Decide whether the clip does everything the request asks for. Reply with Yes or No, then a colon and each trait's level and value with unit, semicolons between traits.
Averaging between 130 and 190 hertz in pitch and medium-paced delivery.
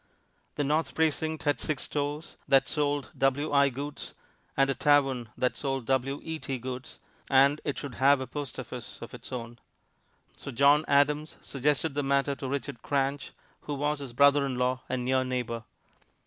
Yes: medium, 140 Hz; average, 165 wpm